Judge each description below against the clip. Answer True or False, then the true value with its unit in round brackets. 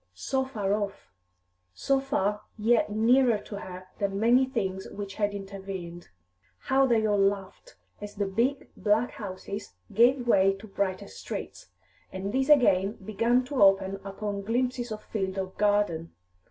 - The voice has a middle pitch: False (205 Hz)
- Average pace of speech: True (150 wpm)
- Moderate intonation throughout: True (3.5 semitones)